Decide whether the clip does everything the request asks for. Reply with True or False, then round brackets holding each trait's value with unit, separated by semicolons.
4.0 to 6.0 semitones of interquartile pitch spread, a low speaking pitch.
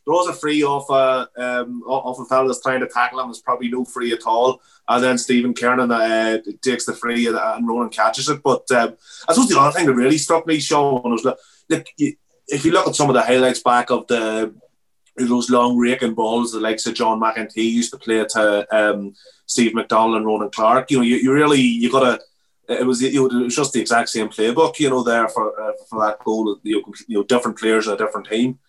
False (2.7 semitones; 120 Hz)